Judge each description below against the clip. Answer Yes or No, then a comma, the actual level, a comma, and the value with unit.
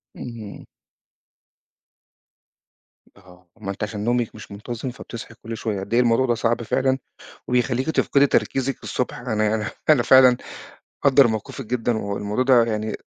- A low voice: Yes, low, 115 Hz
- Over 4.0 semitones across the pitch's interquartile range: No, average, 3.0 semitones